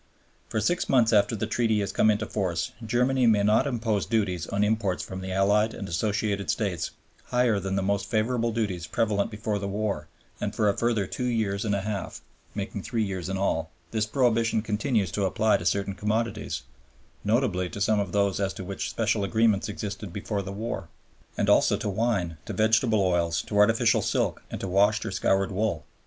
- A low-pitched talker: Yes, low, 105 Hz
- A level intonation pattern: Yes, narrow, 2.3 semitones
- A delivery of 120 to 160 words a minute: No, average, 195 wpm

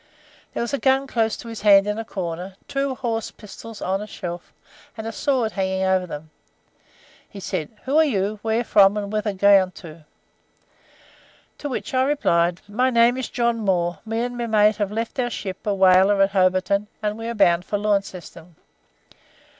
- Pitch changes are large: No, average, 3.5 semitones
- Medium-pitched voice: No, high, 210 Hz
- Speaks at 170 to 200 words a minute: Yes, average, 185 wpm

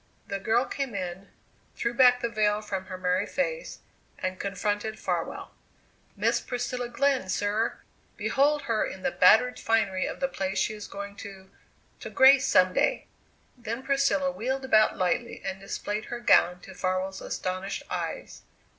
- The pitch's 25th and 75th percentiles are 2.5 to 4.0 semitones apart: No, average, 4.7 semitones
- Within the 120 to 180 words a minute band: Yes, average, 155 wpm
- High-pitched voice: Yes, high, 215 Hz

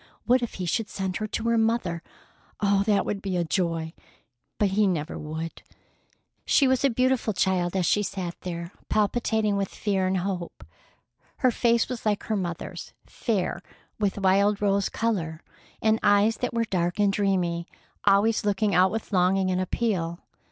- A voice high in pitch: Yes, high, 200 Hz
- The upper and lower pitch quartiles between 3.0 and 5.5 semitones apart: Yes, average, 3.4 semitones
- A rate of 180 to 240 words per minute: No, average, 165 wpm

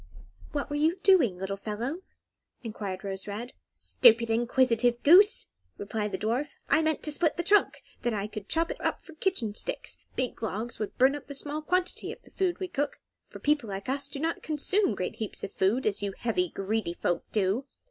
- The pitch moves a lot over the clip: Yes, wide, 6.6 semitones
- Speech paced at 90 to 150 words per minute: No, average, 200 wpm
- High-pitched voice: Yes, high, 240 Hz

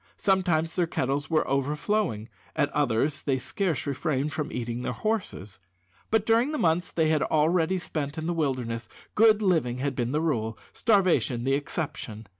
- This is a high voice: No, medium, 150 Hz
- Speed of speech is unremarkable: Yes, average, 165 wpm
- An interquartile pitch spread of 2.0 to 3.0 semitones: No, wide, 5.5 semitones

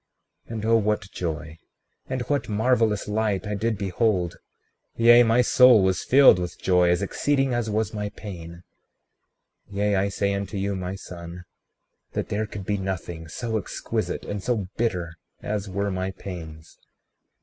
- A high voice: No, low, 100 Hz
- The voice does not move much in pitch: No, average, 3.4 semitones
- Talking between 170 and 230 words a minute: No, average, 160 wpm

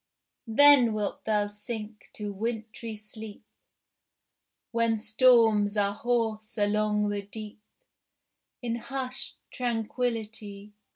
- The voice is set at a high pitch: Yes, high, 220 Hz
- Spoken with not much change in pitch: Yes, narrow, 1.9 semitones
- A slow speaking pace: Yes, slow, 95 wpm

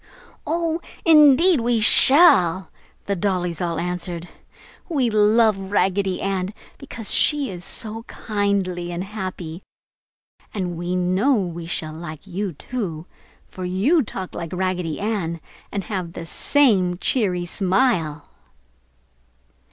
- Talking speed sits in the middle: No, slow, 120 wpm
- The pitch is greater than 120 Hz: Yes, high, 190 Hz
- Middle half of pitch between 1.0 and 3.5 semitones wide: No, average, 4.1 semitones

